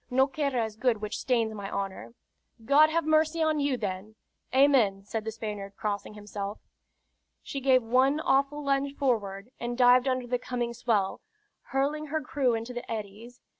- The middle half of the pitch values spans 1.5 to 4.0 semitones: No, average, 4.4 semitones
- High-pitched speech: Yes, high, 245 Hz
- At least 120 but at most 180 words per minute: Yes, average, 170 wpm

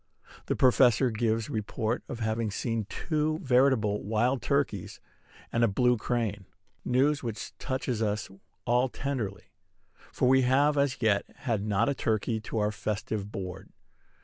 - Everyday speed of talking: Yes, average, 145 wpm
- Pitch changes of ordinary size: Yes, average, 3.5 semitones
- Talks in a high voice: No, low, 115 Hz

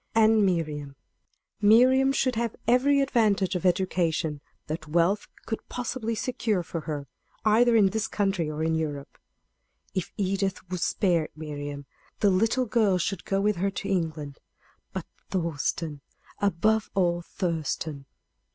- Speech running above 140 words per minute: No, slow, 135 wpm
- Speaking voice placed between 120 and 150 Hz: No, high, 190 Hz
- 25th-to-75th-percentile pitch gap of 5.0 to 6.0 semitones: Yes, average, 5.3 semitones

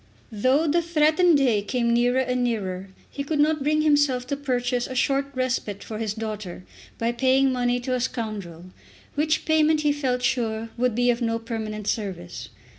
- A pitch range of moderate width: Yes, average, 4.0 semitones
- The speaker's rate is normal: Yes, average, 180 wpm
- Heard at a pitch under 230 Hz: No, very high, 250 Hz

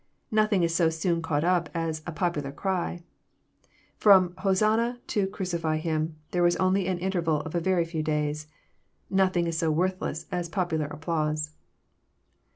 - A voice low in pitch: No, medium, 170 Hz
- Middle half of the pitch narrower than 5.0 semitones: Yes, average, 2.9 semitones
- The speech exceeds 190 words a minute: No, average, 165 wpm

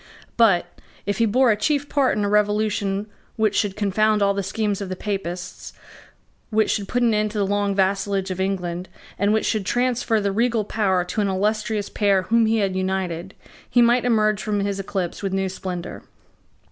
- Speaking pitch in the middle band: No, high, 205 Hz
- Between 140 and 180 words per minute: No, average, 195 wpm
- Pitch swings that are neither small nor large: No, narrow, 2.2 semitones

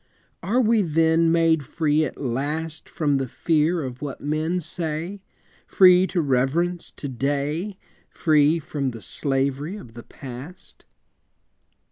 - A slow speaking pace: Yes, slow, 130 wpm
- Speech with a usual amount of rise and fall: Yes, average, 3.5 semitones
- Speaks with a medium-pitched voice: Yes, medium, 155 Hz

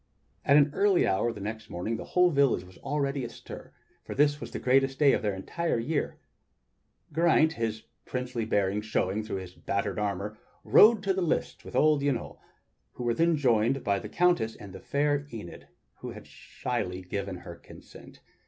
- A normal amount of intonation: No, wide, 6.3 semitones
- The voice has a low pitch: Yes, low, 120 Hz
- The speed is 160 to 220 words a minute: Yes, average, 180 wpm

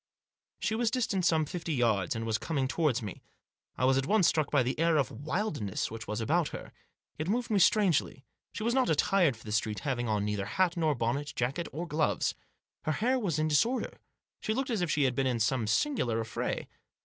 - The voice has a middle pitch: Yes, medium, 150 Hz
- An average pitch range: No, wide, 7.4 semitones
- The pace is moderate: No, fast, 220 wpm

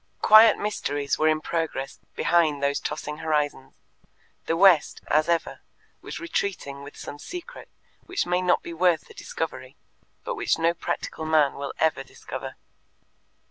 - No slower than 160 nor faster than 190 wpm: No, average, 145 wpm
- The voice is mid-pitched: Yes, medium, 160 Hz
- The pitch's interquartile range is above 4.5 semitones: No, average, 3.8 semitones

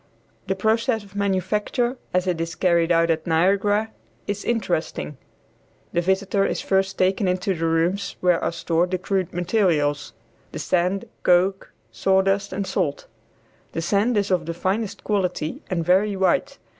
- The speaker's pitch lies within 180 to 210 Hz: Yes, high, 190 Hz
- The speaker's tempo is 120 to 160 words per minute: Yes, average, 155 wpm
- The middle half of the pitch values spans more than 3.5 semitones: No, average, 2.7 semitones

